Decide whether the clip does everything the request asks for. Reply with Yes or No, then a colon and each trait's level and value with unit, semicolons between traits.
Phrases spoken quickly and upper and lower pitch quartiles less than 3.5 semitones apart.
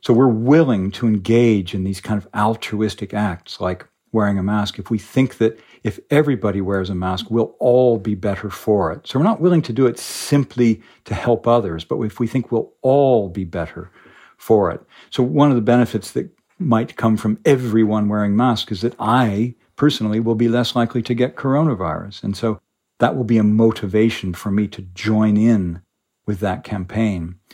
No: average, 195 wpm; average, 2.9 semitones